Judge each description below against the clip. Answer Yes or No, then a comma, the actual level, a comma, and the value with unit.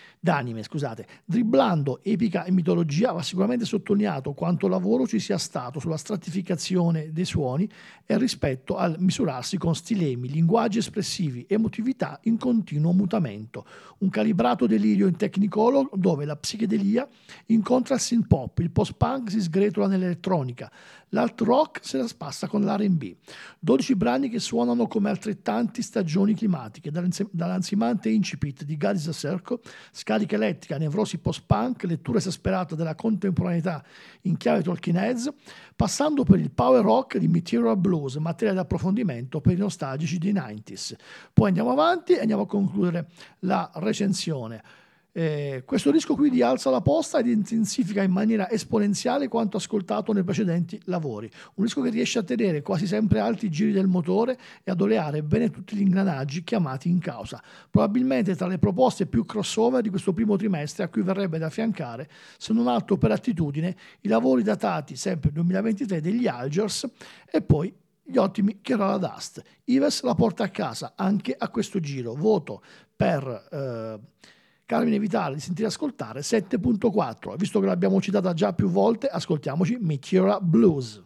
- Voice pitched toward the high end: Yes, high, 195 Hz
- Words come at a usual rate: Yes, average, 155 wpm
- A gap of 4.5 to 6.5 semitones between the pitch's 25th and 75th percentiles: Yes, average, 4.8 semitones